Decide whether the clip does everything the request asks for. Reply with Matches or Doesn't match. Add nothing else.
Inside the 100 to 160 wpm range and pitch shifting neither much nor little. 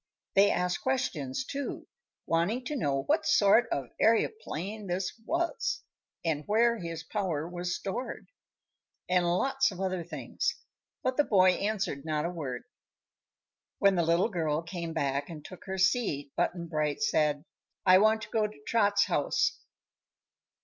Matches